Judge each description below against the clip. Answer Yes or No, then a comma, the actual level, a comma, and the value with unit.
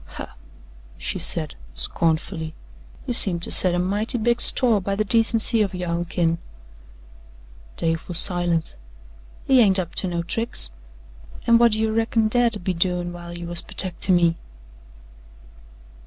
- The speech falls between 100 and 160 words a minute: Yes, average, 155 wpm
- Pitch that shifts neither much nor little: Yes, average, 4.4 semitones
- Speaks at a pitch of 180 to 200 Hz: Yes, medium, 185 Hz